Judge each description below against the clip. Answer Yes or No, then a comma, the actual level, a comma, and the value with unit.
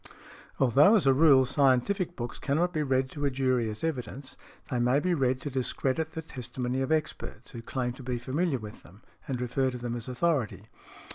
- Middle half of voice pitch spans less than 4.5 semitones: Yes, average, 3.1 semitones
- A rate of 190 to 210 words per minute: Yes, average, 200 wpm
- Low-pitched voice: Yes, low, 130 Hz